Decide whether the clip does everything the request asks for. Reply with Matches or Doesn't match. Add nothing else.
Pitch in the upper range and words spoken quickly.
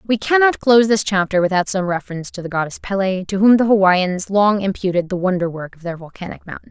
Matches